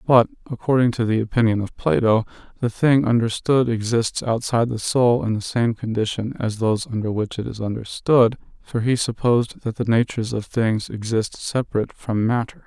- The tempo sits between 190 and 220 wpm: No, average, 175 wpm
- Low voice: Yes, low, 115 Hz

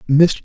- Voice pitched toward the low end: No, medium, 155 Hz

